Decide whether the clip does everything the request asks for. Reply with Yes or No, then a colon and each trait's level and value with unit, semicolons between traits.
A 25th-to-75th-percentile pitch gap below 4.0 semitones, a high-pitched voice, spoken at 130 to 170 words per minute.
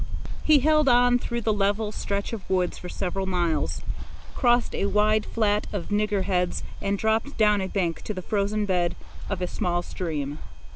No: average, 3.1 semitones; high, 205 Hz; average, 180 wpm